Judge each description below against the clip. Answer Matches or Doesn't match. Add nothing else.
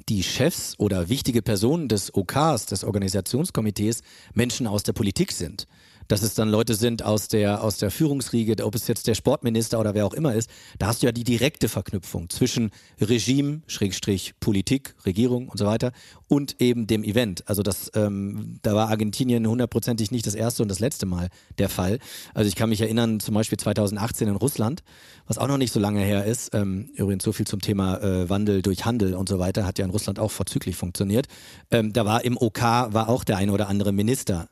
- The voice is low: Matches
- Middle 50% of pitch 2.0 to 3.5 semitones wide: Matches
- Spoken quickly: Matches